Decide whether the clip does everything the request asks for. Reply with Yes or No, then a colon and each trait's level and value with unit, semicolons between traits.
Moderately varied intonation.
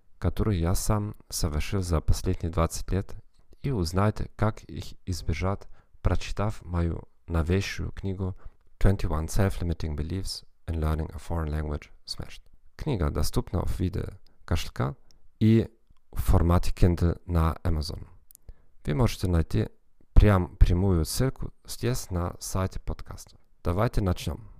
Yes: average, 3.6 semitones